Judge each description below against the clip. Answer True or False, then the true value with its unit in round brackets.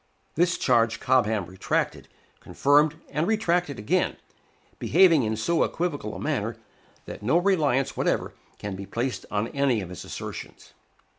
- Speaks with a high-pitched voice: False (135 Hz)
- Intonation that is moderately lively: False (7.5 semitones)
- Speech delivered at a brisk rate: False (140 wpm)